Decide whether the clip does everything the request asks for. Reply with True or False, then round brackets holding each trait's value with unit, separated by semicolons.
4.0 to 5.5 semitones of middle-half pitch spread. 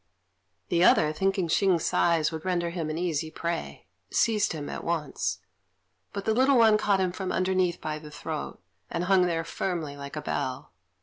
False (3.2 semitones)